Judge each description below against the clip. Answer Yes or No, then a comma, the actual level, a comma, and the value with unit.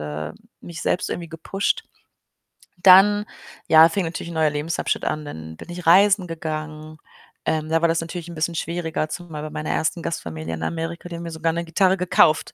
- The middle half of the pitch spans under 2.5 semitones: Yes, narrow, 2.1 semitones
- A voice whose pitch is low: No, medium, 165 Hz